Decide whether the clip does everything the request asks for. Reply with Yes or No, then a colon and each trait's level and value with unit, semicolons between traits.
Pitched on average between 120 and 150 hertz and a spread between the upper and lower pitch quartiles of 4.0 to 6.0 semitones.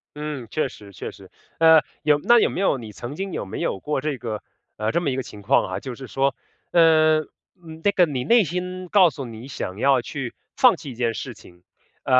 Yes: medium, 140 Hz; average, 5.1 semitones